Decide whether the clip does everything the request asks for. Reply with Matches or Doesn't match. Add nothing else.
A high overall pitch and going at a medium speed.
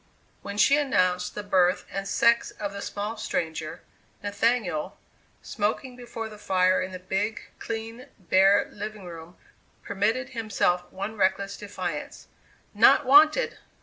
Doesn't match